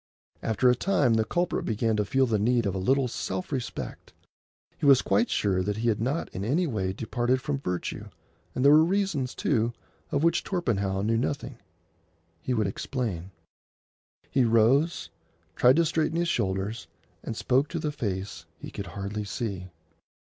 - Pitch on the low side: Yes, low, 120 Hz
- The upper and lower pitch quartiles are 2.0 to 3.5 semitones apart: No, wide, 5.6 semitones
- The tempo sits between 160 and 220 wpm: Yes, average, 170 wpm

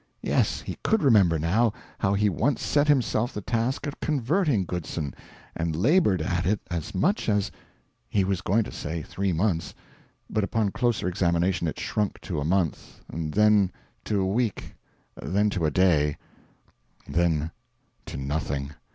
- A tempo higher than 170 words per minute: No, average, 155 wpm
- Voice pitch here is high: No, very low, 95 Hz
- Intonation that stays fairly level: No, average, 5.0 semitones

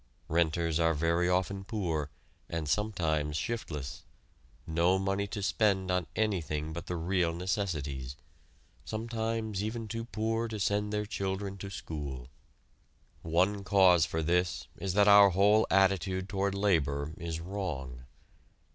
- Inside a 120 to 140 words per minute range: Yes, slow, 135 wpm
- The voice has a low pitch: Yes, very low, 95 Hz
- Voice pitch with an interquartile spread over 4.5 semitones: No, average, 3.9 semitones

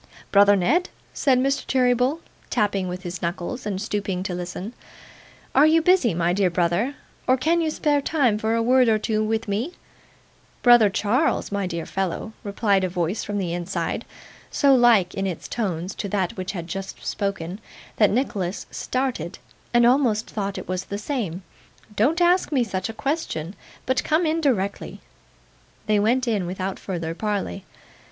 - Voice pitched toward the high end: Yes, high, 210 Hz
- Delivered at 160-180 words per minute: Yes, average, 170 wpm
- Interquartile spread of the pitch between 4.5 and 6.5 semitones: Yes, wide, 5.4 semitones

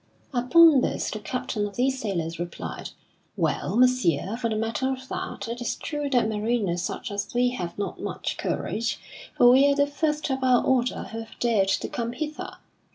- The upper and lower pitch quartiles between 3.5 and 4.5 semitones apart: Yes, average, 4.0 semitones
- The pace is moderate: Yes, average, 190 wpm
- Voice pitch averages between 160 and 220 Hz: No, high, 240 Hz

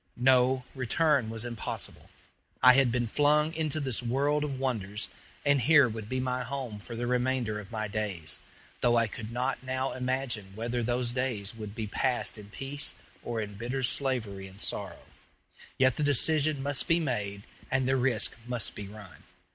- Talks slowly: No, average, 175 wpm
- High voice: No, low, 125 Hz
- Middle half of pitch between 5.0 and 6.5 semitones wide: No, average, 3.5 semitones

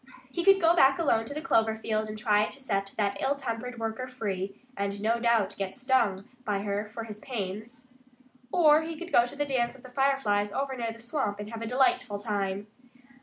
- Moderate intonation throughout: Yes, average, 4.4 semitones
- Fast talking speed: Yes, fast, 215 wpm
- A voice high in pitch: Yes, high, 230 Hz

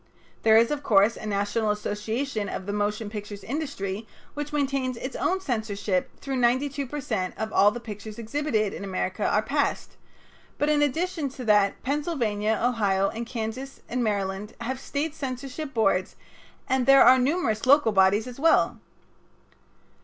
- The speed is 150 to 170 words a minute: Yes, average, 160 wpm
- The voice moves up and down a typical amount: Yes, average, 4.9 semitones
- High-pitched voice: Yes, high, 235 Hz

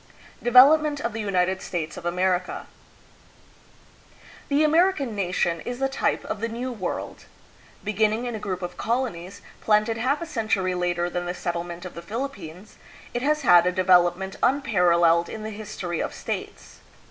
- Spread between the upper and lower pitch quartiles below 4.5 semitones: No, wide, 5.5 semitones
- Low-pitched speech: No, high, 200 Hz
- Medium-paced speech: Yes, average, 165 wpm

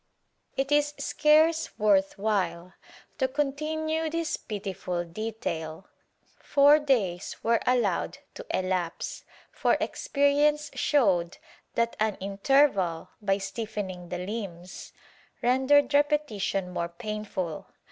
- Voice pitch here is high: Yes, high, 215 Hz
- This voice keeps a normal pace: No, slow, 105 wpm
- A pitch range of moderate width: No, wide, 7.5 semitones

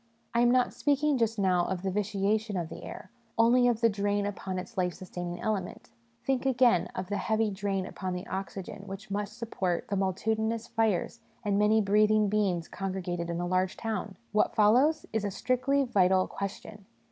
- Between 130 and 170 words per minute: No, average, 195 wpm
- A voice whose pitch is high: Yes, high, 205 Hz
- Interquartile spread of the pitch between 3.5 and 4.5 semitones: No, average, 3.0 semitones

